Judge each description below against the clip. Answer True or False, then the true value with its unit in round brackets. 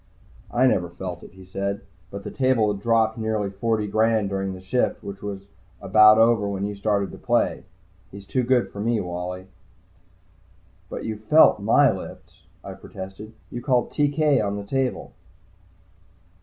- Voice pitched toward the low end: True (105 Hz)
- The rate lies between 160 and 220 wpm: True (165 wpm)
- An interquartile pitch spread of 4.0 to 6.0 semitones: False (3.0 semitones)